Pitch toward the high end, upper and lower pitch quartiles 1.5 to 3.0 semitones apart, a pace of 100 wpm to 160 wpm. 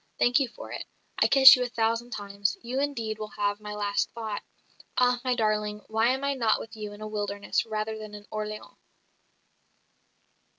No: high, 220 Hz; narrow, 2.6 semitones; average, 185 wpm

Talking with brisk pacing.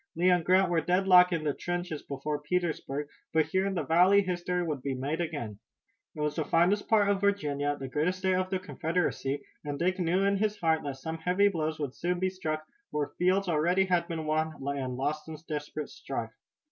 Yes: fast, 210 wpm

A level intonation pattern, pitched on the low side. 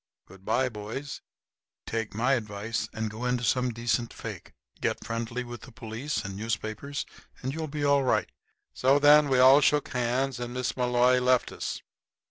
No: average, 3.0 semitones; low, 125 Hz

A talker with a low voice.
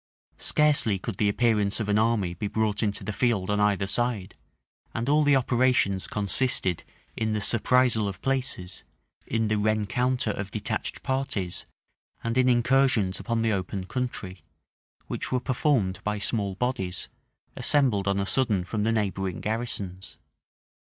Yes: low, 110 Hz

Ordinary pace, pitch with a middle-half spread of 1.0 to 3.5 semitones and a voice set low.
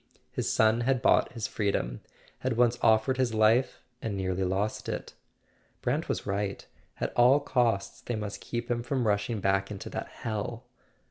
Yes: average, 165 wpm; average, 3.1 semitones; low, 110 Hz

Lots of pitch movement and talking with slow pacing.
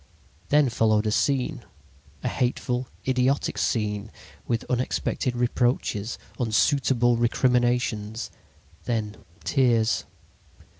No: narrow, 2.4 semitones; slow, 85 wpm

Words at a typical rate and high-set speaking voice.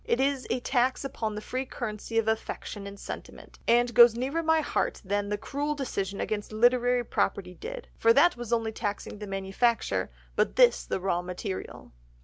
Yes: average, 180 wpm; high, 235 Hz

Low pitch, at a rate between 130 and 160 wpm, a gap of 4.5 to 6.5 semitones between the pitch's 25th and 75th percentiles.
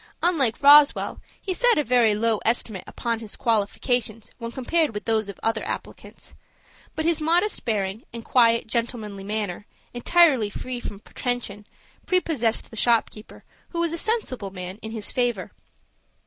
No: high, 230 Hz; average, 155 wpm; average, 4.8 semitones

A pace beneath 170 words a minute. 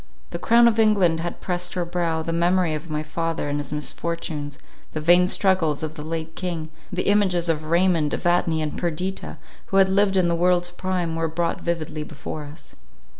No: average, 190 wpm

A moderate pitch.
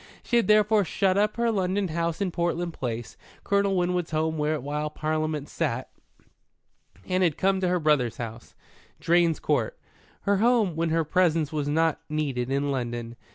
Yes: medium, 165 Hz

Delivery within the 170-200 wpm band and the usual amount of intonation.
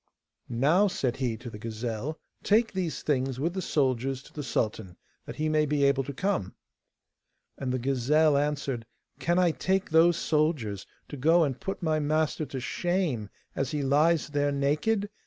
Yes: average, 175 wpm; average, 4.0 semitones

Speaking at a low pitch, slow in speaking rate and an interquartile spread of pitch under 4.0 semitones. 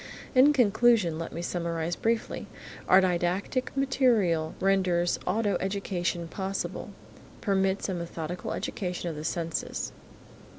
No: medium, 185 Hz; slow, 115 wpm; average, 3.2 semitones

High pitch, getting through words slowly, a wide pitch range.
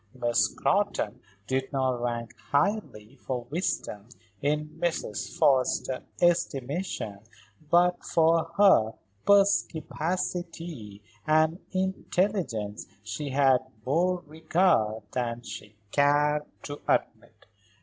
No: medium, 145 Hz; slow, 90 wpm; wide, 6.2 semitones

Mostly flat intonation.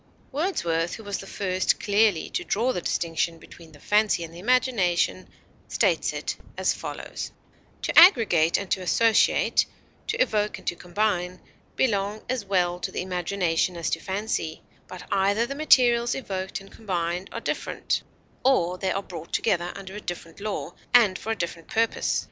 No: average, 4.0 semitones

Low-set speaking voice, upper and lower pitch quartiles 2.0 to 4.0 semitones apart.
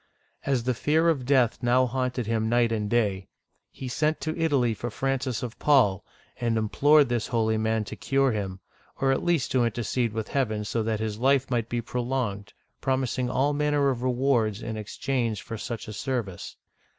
Yes: low, 120 Hz; average, 3.3 semitones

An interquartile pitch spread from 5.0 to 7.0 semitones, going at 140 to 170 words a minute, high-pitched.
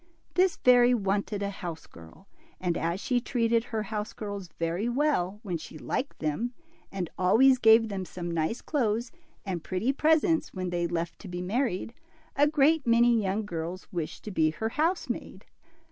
Yes: wide, 5.4 semitones; average, 165 wpm; high, 210 Hz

